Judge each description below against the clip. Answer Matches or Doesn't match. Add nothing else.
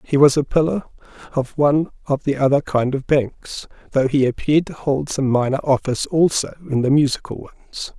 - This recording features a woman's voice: Doesn't match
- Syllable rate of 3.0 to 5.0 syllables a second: Doesn't match